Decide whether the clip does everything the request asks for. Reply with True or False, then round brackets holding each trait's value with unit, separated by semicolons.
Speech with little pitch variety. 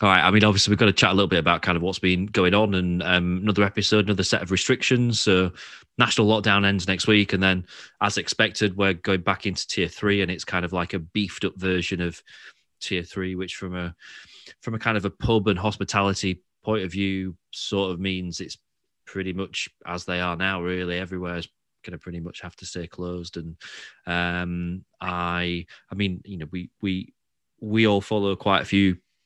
True (2.2 semitones)